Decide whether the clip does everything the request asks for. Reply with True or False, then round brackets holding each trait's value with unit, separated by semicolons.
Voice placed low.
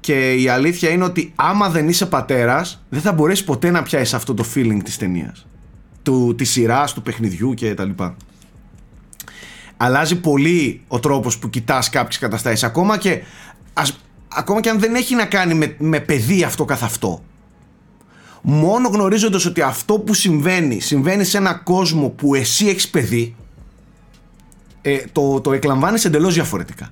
False (145 Hz)